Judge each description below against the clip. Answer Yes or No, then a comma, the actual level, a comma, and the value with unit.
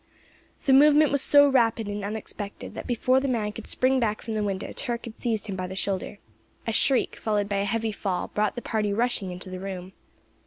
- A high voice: Yes, high, 215 Hz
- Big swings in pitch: No, average, 3.3 semitones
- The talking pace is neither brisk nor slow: No, fast, 220 wpm